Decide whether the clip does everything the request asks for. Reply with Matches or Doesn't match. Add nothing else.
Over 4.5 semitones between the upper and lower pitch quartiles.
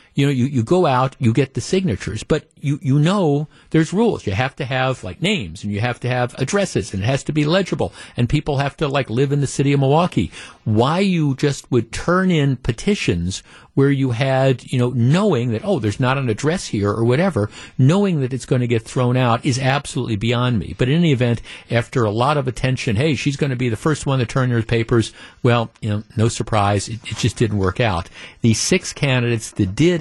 Doesn't match